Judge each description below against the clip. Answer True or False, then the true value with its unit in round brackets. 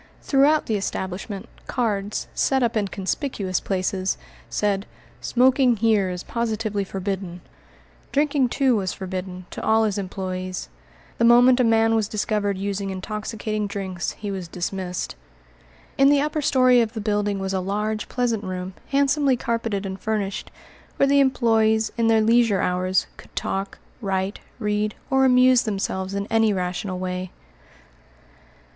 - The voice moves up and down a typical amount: True (3.5 semitones)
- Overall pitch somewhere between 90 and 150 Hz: False (210 Hz)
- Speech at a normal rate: True (145 wpm)